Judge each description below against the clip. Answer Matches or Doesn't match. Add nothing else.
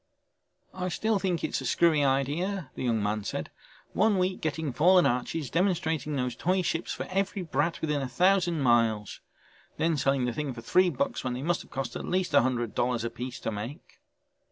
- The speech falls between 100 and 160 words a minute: Doesn't match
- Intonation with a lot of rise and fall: Matches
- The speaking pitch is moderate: Matches